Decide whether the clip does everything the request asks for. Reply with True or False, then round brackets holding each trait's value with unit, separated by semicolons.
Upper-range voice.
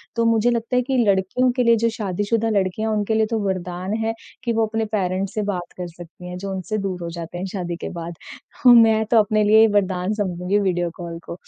True (200 Hz)